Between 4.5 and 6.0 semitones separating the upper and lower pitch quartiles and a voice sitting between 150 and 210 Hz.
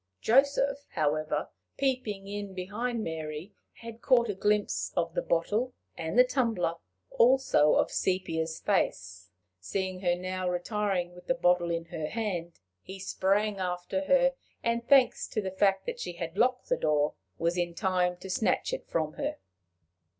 Yes: average, 4.8 semitones; high, 190 Hz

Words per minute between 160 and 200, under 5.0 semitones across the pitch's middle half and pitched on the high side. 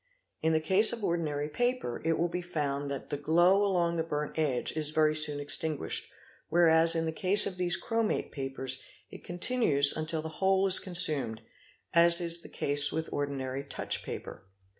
No: average, 180 wpm; average, 3.5 semitones; medium, 160 Hz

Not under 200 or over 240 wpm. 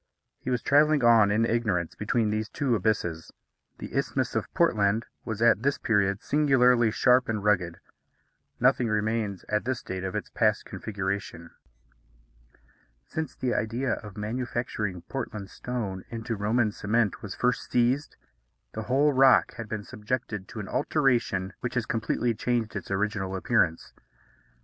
No: average, 145 wpm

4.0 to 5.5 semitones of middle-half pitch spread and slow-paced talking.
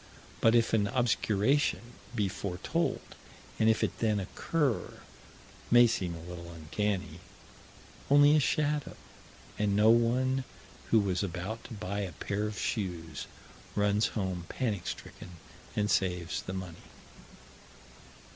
Yes: average, 4.3 semitones; slow, 130 wpm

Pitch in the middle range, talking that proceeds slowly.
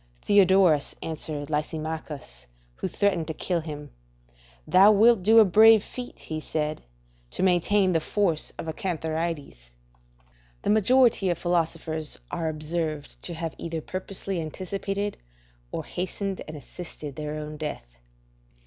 Yes: medium, 165 Hz; slow, 130 wpm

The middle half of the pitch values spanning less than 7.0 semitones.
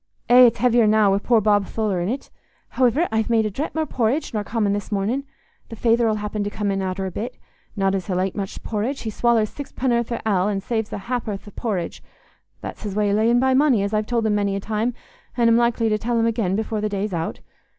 Yes: average, 2.8 semitones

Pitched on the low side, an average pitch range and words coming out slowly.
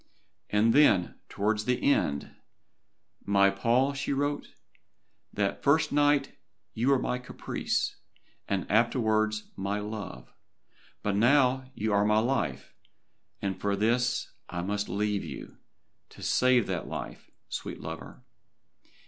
Yes: low, 110 Hz; average, 4.1 semitones; slow, 125 wpm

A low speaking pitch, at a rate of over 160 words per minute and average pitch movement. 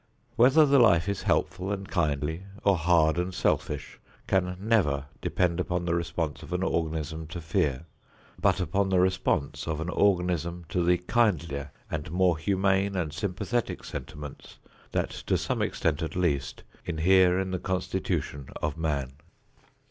No: very low, 90 Hz; average, 150 wpm; average, 3.2 semitones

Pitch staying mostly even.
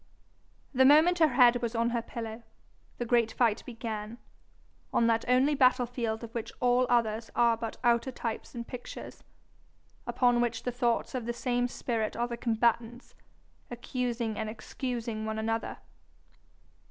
Yes: narrow, 1.5 semitones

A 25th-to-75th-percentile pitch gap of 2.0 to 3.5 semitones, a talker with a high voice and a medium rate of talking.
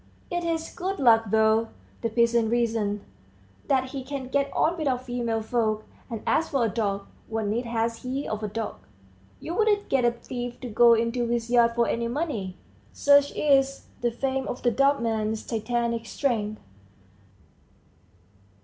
Yes: average, 3.2 semitones; high, 235 Hz; average, 165 wpm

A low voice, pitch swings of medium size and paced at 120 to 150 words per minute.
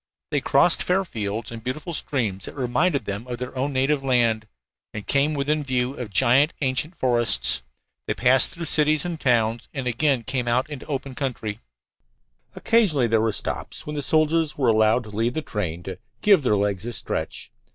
No: low, 130 Hz; average, 4.5 semitones; average, 190 wpm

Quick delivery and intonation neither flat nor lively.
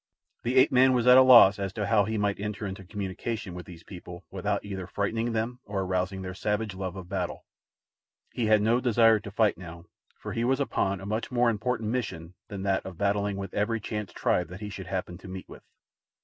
Yes: fast, 220 wpm; average, 3.2 semitones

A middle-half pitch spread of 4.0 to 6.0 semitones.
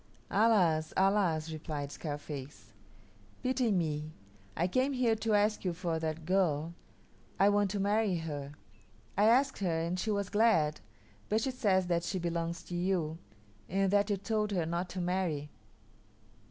Yes: average, 4.3 semitones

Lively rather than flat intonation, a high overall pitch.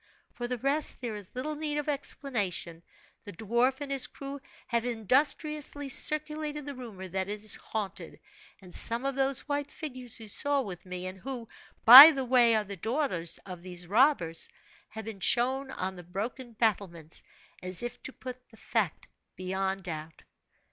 Yes: wide, 6.2 semitones; high, 235 Hz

